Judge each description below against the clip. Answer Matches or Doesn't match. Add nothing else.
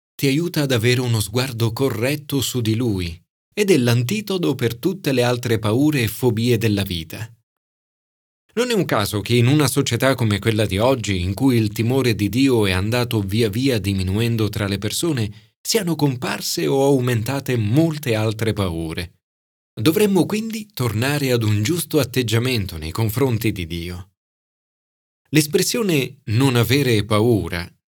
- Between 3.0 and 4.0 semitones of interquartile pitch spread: Doesn't match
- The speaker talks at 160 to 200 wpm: Doesn't match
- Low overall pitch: Matches